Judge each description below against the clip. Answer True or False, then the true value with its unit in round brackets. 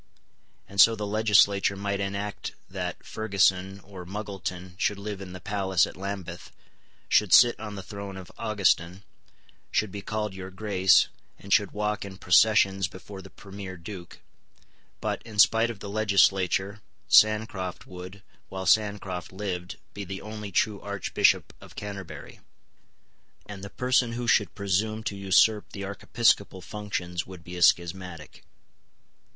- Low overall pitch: True (100 Hz)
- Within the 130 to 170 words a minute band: True (145 wpm)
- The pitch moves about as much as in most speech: False (1.9 semitones)